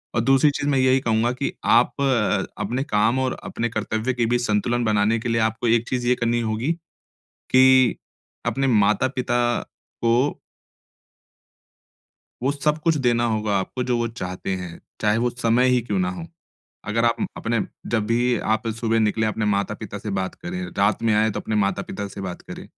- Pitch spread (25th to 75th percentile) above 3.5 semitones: No, average, 2.8 semitones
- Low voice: Yes, low, 115 Hz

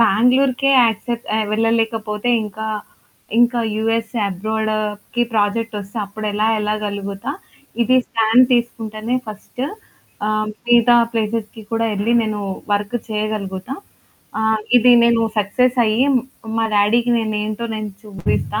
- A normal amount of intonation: No, narrow, 1.9 semitones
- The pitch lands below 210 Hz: No, high, 220 Hz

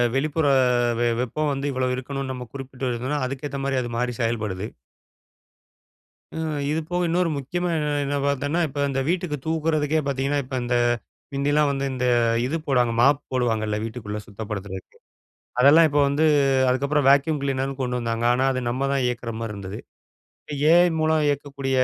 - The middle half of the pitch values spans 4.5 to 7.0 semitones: No, average, 3.0 semitones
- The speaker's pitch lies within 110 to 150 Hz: Yes, low, 135 Hz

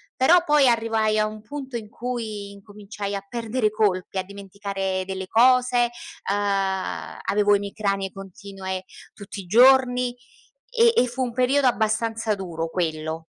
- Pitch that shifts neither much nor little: Yes, average, 3.8 semitones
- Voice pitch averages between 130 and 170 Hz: No, high, 210 Hz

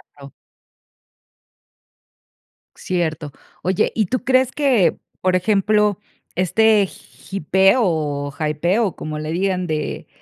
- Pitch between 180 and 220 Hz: Yes, medium, 185 Hz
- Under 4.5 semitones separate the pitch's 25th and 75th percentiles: No, average, 5.1 semitones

